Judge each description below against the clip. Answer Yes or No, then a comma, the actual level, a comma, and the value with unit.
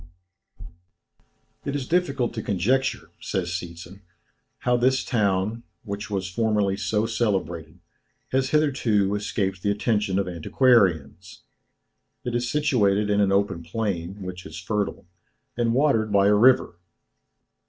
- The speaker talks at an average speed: No, slow, 125 wpm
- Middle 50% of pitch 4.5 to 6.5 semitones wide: No, average, 4.1 semitones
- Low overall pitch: Yes, low, 105 Hz